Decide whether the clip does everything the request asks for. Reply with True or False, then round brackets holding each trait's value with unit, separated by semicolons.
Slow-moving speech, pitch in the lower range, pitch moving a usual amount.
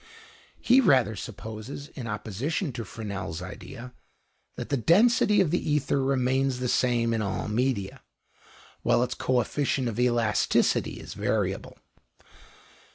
True (125 wpm; 125 Hz; 3.7 semitones)